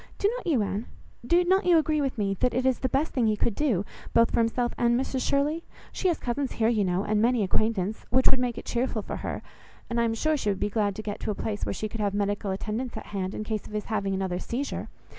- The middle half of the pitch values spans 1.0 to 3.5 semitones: No, average, 4.1 semitones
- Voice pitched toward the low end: No, high, 230 Hz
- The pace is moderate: No, fast, 275 wpm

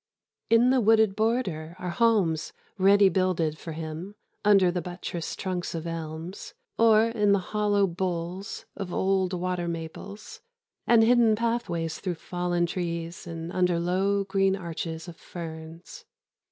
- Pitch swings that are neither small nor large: Yes, average, 3.4 semitones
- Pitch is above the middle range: No, medium, 180 Hz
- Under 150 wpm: Yes, average, 140 wpm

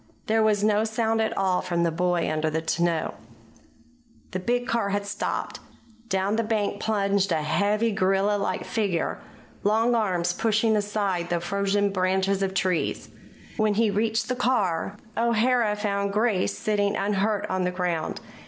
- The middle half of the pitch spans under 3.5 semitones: Yes, average, 2.9 semitones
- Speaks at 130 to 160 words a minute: Yes, average, 155 wpm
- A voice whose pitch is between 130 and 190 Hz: No, high, 200 Hz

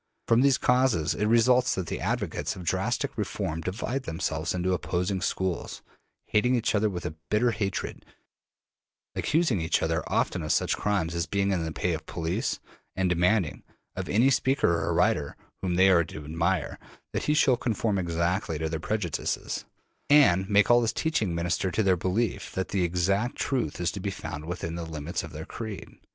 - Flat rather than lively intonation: No, average, 4.8 semitones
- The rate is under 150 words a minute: No, average, 185 wpm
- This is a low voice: Yes, very low, 95 Hz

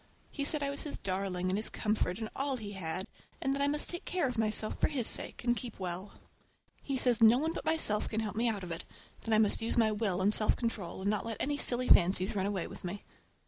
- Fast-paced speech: Yes, fast, 260 wpm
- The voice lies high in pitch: Yes, high, 220 Hz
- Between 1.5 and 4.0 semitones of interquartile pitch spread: No, average, 4.6 semitones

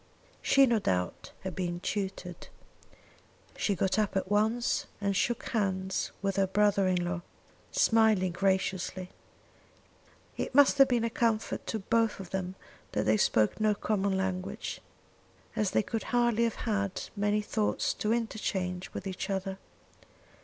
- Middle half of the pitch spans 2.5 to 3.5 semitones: Yes, average, 2.8 semitones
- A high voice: Yes, high, 200 Hz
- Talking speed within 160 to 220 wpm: No, average, 145 wpm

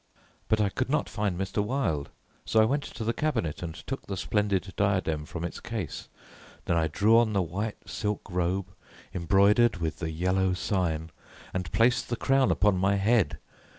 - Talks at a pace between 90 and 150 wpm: No, average, 180 wpm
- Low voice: Yes, low, 100 Hz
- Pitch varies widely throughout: No, average, 4.0 semitones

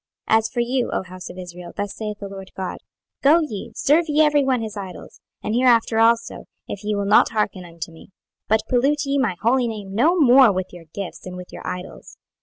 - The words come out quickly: Yes, fast, 220 wpm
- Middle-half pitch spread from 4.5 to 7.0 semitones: Yes, average, 5.2 semitones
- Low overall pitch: No, high, 220 Hz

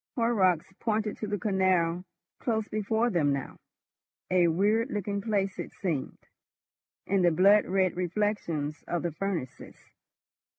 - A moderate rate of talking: No, slow, 130 wpm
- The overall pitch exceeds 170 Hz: Yes, high, 190 Hz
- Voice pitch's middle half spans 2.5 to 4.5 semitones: Yes, average, 3.5 semitones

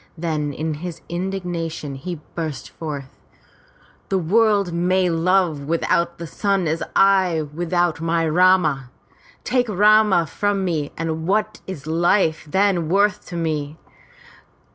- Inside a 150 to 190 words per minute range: No, slow, 135 wpm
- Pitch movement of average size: Yes, average, 3.2 semitones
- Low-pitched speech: No, medium, 170 Hz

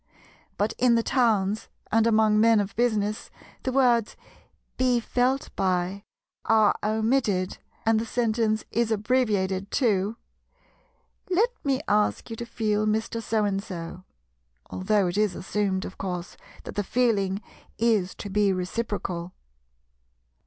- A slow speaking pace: Yes, slow, 130 wpm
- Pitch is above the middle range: Yes, high, 215 Hz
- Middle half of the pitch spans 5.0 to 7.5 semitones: No, average, 2.9 semitones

